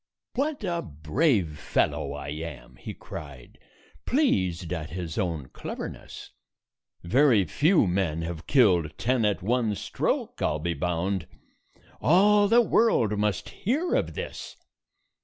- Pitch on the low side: Yes, very low, 95 Hz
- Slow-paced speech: Yes, slow, 130 wpm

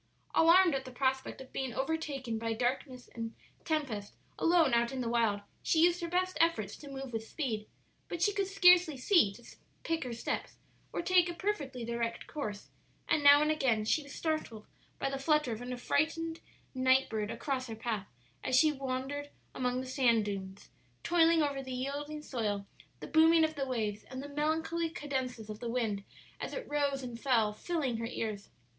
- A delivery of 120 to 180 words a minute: No, average, 190 wpm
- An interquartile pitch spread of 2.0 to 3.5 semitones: No, average, 5.2 semitones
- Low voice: No, very high, 265 Hz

